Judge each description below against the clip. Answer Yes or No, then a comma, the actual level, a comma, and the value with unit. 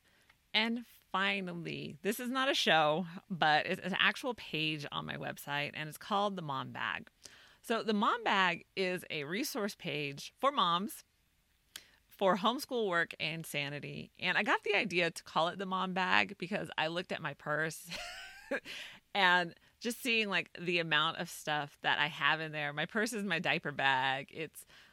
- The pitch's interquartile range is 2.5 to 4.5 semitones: No, average, 5.0 semitones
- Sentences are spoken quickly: No, average, 175 wpm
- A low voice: No, medium, 180 Hz